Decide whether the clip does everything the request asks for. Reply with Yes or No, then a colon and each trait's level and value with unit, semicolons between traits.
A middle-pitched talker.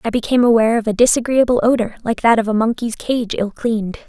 No: high, 230 Hz